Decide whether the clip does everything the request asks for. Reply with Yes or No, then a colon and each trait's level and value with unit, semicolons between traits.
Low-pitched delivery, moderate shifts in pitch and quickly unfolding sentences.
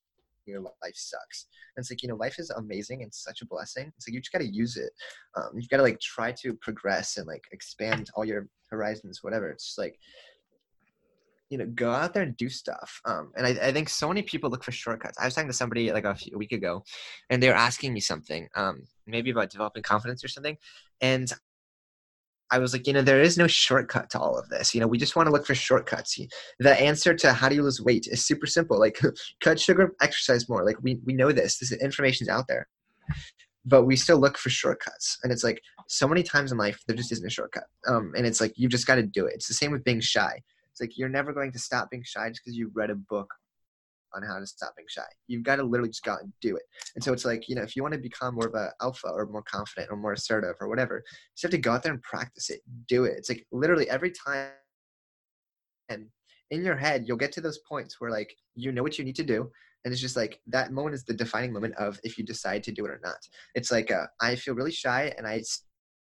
Yes: low, 125 Hz; average, 3.3 semitones; fast, 260 wpm